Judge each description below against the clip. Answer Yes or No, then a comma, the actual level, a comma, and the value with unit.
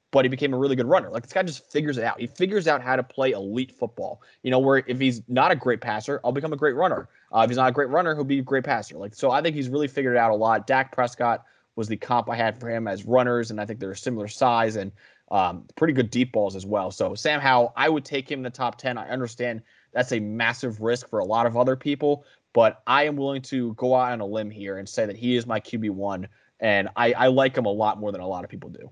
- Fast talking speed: Yes, fast, 290 wpm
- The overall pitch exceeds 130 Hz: No, low, 125 Hz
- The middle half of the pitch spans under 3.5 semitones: Yes, average, 3.1 semitones